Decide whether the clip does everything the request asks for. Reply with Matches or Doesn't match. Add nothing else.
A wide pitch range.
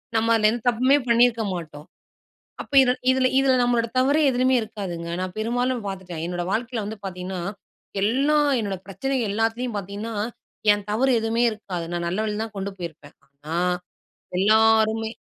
Doesn't match